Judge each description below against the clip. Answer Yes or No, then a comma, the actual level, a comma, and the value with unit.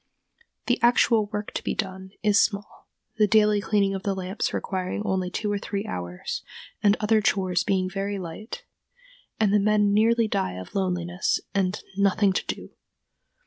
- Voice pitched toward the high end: Yes, high, 200 Hz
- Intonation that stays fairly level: Yes, narrow, 2.1 semitones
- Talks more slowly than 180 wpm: Yes, average, 165 wpm